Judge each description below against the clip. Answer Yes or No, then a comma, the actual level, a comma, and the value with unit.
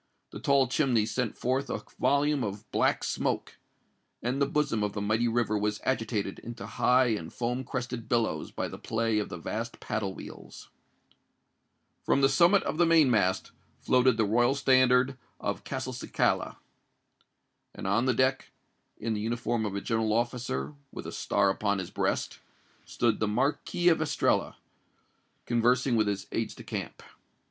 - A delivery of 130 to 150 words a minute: No, average, 165 wpm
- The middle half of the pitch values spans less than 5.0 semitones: Yes, average, 3.5 semitones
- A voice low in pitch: Yes, low, 120 Hz